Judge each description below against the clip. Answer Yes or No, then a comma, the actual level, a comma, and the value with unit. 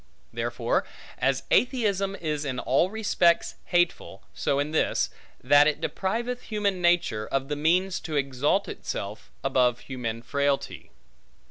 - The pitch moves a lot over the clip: Yes, wide, 6.0 semitones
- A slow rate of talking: Yes, slow, 130 wpm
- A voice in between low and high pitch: Yes, medium, 150 Hz